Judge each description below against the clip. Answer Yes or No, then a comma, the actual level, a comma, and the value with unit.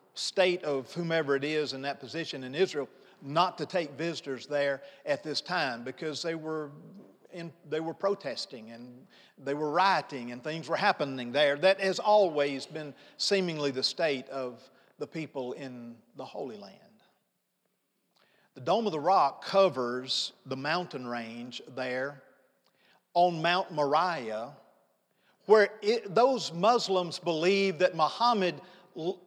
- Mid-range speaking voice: Yes, medium, 155 Hz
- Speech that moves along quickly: No, average, 140 wpm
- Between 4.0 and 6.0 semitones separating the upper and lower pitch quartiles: Yes, average, 5.1 semitones